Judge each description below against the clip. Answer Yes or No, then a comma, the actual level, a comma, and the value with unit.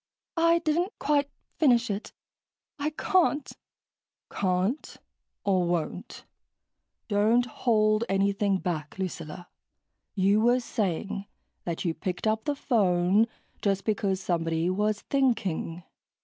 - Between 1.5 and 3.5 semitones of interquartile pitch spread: No, average, 4.7 semitones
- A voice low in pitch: No, high, 205 Hz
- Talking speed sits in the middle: No, slow, 105 wpm